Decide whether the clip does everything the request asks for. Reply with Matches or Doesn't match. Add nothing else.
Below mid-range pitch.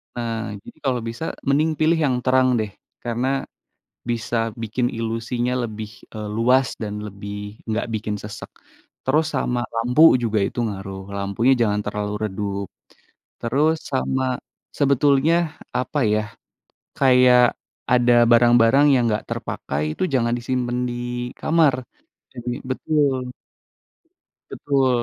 Matches